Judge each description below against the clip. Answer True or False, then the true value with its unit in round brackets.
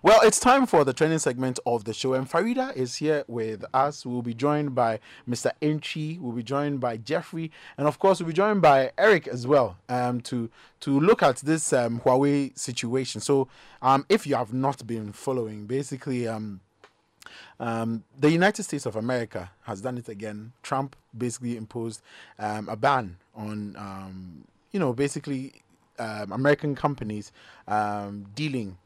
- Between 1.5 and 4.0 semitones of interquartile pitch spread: False (4.5 semitones)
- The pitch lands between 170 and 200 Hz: False (130 Hz)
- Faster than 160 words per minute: True (170 wpm)